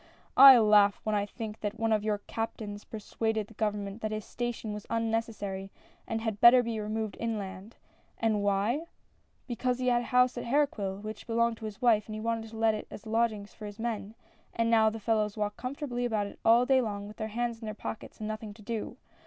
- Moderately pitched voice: No, high, 220 Hz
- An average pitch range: No, narrow, 1.9 semitones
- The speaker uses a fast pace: Yes, fast, 225 wpm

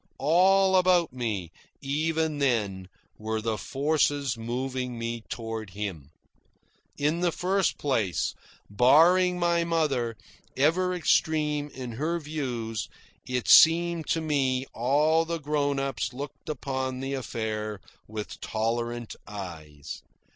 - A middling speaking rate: No, slow, 115 wpm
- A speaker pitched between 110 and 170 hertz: Yes, low, 135 Hz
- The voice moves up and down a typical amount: No, wide, 5.8 semitones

